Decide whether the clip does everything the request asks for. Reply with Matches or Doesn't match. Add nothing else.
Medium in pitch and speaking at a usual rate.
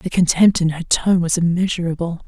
Matches